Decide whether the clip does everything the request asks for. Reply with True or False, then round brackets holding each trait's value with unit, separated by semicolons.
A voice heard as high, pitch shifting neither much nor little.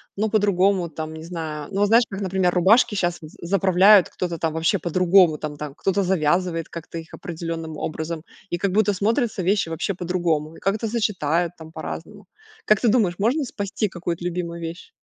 False (180 Hz; 3.4 semitones)